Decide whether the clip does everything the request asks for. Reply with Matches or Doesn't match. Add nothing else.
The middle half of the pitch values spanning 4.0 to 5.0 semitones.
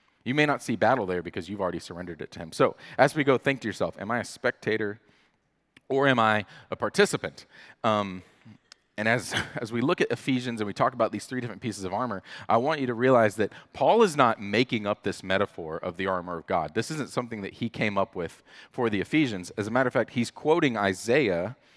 Matches